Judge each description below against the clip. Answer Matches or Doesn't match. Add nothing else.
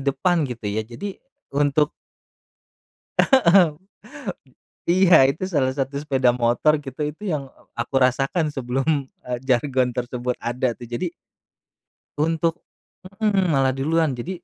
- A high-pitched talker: Doesn't match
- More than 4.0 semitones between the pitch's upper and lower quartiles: Matches